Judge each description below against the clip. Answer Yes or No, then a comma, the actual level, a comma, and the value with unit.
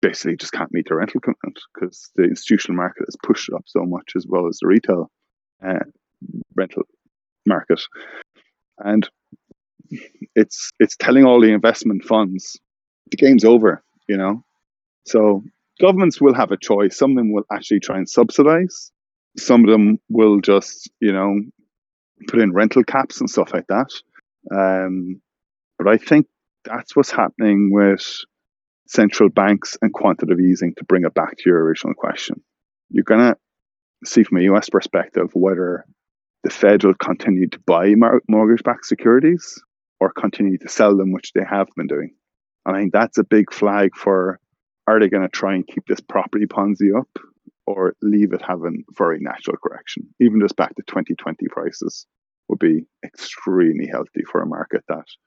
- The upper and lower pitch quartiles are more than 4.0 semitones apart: No, average, 3.2 semitones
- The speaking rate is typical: Yes, average, 170 wpm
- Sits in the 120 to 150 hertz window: No, low, 105 Hz